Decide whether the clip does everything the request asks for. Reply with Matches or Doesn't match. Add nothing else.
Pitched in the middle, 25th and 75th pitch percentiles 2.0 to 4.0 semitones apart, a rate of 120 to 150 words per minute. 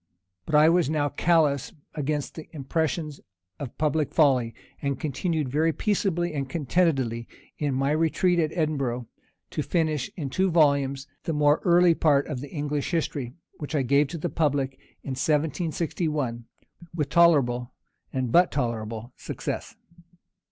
Matches